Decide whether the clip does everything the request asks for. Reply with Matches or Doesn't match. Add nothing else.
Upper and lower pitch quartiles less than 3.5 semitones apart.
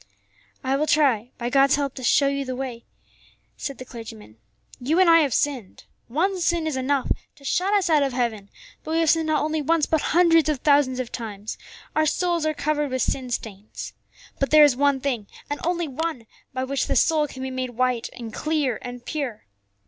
Doesn't match